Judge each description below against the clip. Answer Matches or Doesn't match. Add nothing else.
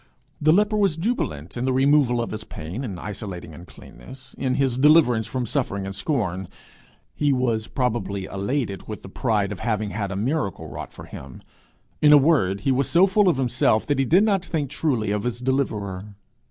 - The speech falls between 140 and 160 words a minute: Doesn't match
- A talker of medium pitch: Doesn't match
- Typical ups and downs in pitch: Doesn't match